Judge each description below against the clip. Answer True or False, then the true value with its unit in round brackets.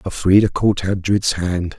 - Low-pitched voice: True (95 Hz)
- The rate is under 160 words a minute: True (135 wpm)